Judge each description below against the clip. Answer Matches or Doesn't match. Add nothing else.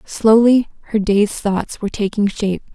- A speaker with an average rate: Matches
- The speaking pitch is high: Matches